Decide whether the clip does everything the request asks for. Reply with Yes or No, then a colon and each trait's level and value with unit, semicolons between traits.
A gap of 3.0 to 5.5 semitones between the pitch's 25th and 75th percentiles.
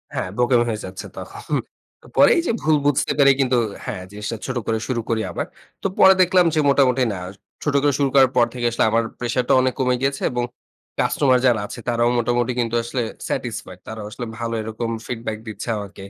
No: narrow, 2.6 semitones